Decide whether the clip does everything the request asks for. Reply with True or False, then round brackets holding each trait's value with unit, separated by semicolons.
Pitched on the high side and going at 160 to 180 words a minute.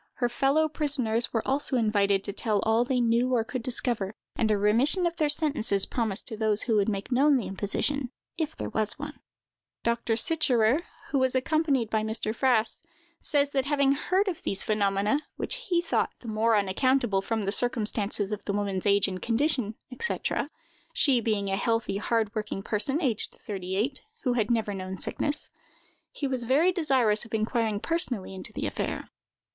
True (230 Hz; 175 wpm)